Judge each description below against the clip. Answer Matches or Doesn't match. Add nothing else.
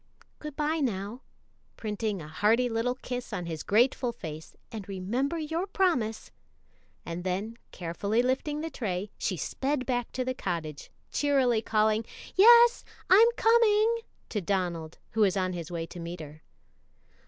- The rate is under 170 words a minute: Matches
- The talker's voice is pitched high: Matches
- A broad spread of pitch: Matches